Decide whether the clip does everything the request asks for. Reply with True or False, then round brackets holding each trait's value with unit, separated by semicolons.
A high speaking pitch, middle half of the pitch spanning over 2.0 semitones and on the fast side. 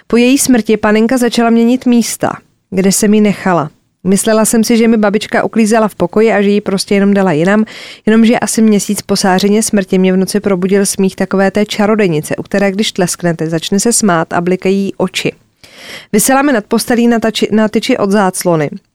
True (210 Hz; 2.7 semitones; 185 wpm)